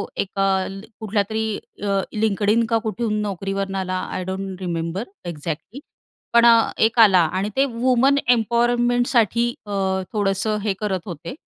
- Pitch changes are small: No, average, 3.3 semitones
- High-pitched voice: Yes, high, 210 Hz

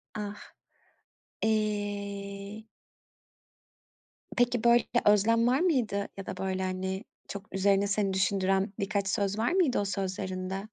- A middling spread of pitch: No, narrow, 2.1 semitones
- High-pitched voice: Yes, high, 200 Hz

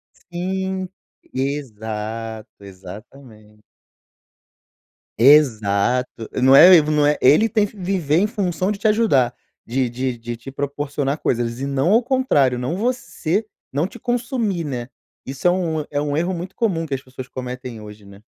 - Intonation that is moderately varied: No, wide, 7.2 semitones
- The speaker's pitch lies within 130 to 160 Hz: Yes, medium, 140 Hz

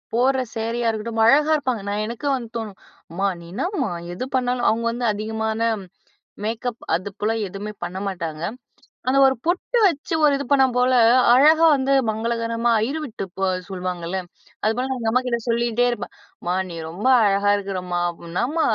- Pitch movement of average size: Yes, average, 4.0 semitones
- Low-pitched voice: No, high, 230 Hz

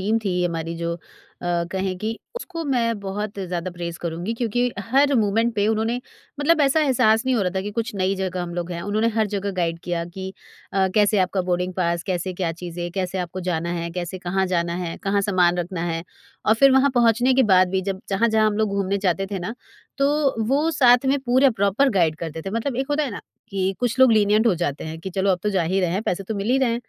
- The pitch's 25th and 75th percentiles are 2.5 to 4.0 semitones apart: No, average, 4.5 semitones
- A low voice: No, high, 195 Hz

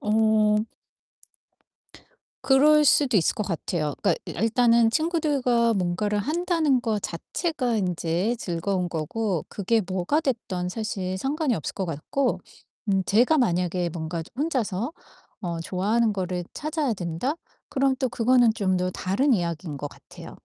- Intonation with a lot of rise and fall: Yes, wide, 6.1 semitones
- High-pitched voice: Yes, high, 215 Hz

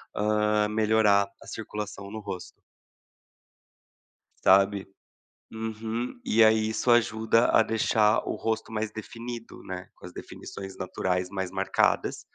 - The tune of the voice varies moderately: No, narrow, 2.0 semitones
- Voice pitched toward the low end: Yes, low, 105 Hz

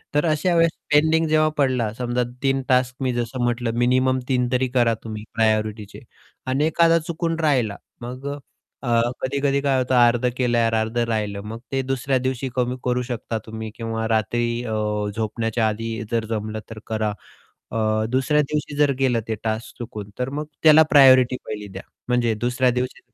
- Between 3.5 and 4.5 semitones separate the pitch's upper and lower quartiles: No, average, 3.0 semitones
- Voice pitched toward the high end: No, low, 125 Hz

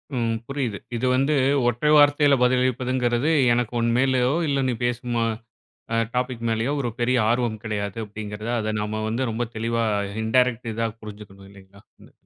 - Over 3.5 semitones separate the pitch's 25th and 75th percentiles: No, average, 2.7 semitones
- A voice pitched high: No, low, 120 Hz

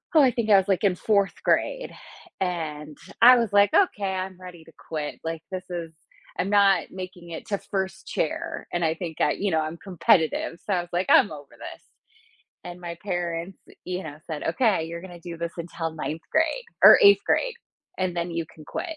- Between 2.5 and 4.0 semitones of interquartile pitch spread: Yes, average, 3.2 semitones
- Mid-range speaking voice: Yes, medium, 180 Hz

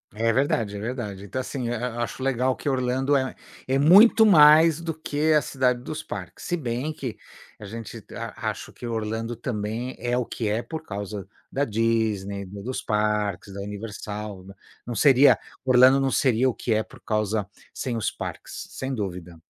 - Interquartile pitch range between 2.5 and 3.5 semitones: No, average, 4.0 semitones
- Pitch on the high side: No, low, 120 Hz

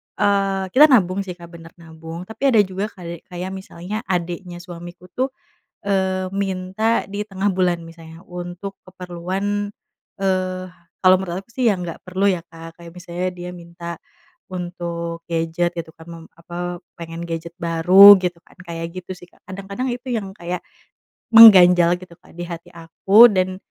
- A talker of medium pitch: Yes, medium, 180 Hz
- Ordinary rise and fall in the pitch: No, narrow, 2.2 semitones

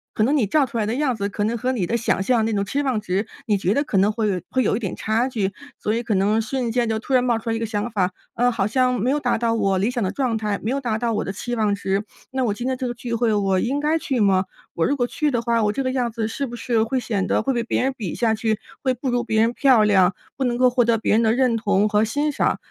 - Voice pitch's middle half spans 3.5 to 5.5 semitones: No, average, 3.0 semitones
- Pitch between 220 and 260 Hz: Yes, high, 230 Hz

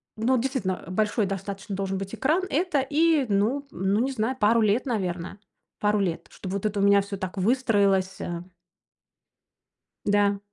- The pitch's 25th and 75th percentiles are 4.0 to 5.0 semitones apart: Yes, average, 4.5 semitones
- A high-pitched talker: Yes, high, 205 Hz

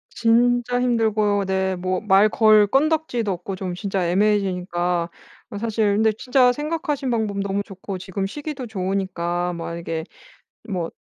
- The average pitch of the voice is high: Yes, high, 205 Hz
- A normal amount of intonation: Yes, average, 3.9 semitones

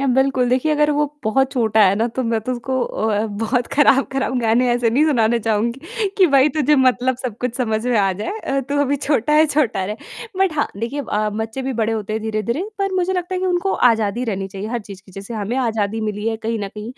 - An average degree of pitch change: Yes, average, 4.2 semitones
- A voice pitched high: Yes, high, 240 Hz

